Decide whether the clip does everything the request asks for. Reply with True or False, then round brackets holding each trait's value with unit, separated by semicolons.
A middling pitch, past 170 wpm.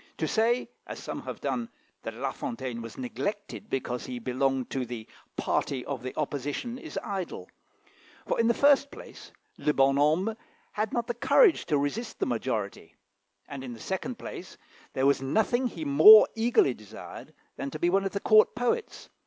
True (150 Hz; 180 wpm)